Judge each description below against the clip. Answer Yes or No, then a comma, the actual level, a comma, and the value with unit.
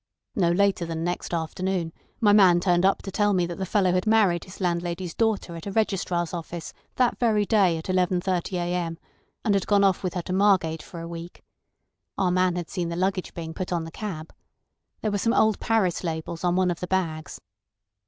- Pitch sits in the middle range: Yes, medium, 180 Hz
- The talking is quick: Yes, fast, 210 wpm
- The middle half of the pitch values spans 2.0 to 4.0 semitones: Yes, narrow, 2.4 semitones